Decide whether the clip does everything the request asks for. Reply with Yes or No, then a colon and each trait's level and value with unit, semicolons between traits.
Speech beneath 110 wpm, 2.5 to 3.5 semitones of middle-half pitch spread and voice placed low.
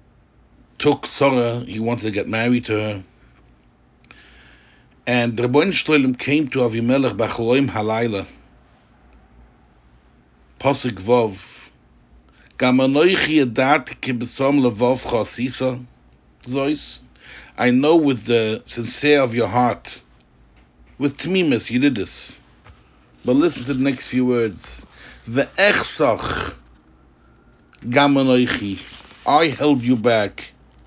No: slow, 95 wpm; average, 4.0 semitones; low, 125 Hz